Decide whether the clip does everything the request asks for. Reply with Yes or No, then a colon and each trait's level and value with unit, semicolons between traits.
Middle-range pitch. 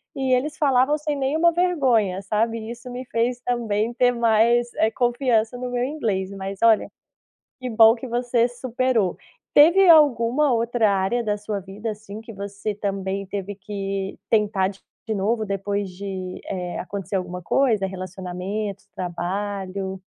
No: high, 220 Hz